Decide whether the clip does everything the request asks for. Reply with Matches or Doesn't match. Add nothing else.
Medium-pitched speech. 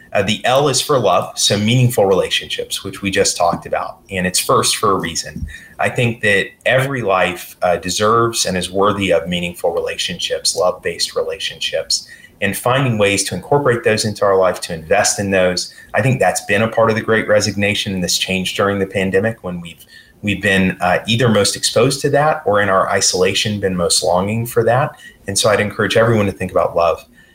Doesn't match